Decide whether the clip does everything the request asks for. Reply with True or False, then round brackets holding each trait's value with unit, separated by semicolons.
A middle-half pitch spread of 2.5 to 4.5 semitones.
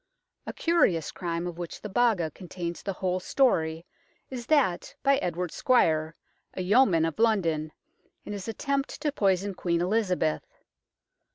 False (5.3 semitones)